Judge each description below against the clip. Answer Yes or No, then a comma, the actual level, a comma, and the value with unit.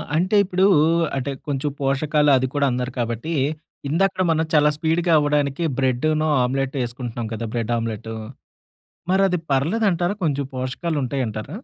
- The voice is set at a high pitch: No, medium, 145 Hz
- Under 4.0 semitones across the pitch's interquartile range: No, average, 4.4 semitones